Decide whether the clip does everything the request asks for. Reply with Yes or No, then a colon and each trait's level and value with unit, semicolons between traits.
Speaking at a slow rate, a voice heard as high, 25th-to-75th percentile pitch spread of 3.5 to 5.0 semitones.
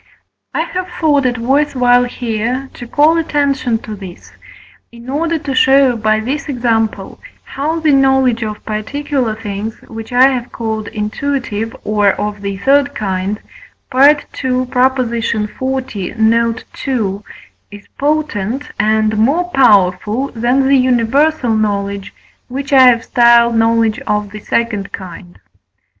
Yes: slow, 130 wpm; high, 235 Hz; average, 4.0 semitones